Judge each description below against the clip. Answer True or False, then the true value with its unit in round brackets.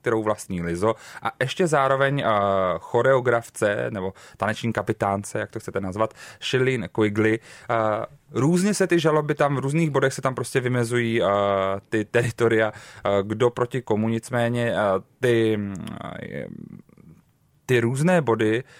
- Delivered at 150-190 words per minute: False (120 wpm)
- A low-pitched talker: True (115 Hz)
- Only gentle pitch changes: False (3.7 semitones)